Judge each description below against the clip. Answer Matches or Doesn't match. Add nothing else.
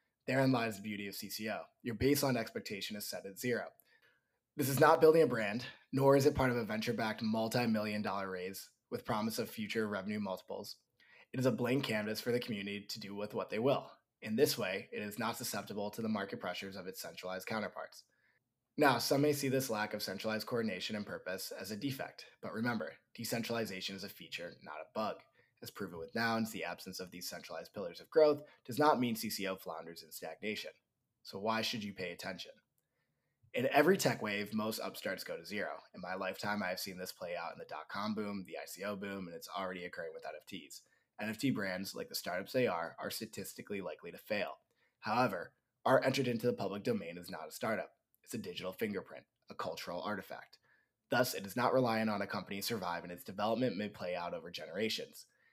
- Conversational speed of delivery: Doesn't match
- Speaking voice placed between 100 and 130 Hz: Matches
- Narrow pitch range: Doesn't match